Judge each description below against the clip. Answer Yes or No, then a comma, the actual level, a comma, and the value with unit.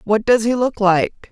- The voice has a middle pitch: No, high, 215 Hz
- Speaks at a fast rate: Yes, fast, 230 wpm